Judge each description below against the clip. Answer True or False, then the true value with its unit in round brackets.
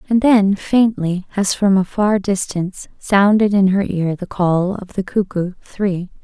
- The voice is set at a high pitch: True (195 Hz)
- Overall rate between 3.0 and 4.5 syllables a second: True (4.0 syllables/s)